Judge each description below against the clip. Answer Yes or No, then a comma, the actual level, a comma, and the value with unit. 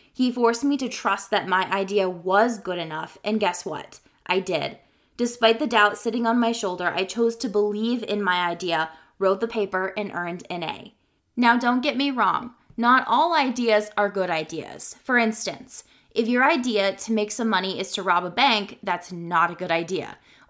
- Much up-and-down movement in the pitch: No, average, 4.2 semitones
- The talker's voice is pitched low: No, high, 210 Hz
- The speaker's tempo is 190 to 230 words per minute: Yes, average, 195 wpm